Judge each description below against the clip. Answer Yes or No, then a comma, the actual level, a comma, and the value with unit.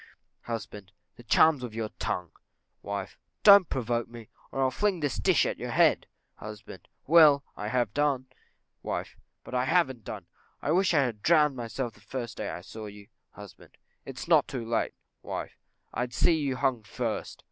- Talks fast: No, average, 175 wpm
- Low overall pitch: Yes, low, 125 Hz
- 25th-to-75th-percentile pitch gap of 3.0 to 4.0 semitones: No, average, 4.8 semitones